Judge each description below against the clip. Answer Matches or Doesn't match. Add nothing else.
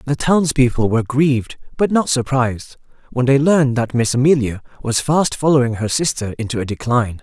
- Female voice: Doesn't match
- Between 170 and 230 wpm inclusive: Matches